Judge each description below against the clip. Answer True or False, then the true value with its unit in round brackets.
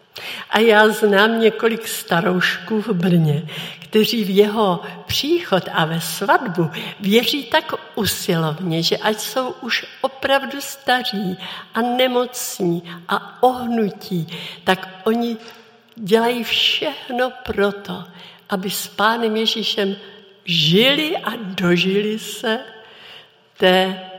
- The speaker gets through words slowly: True (100 wpm)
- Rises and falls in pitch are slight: False (3.6 semitones)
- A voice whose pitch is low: False (210 Hz)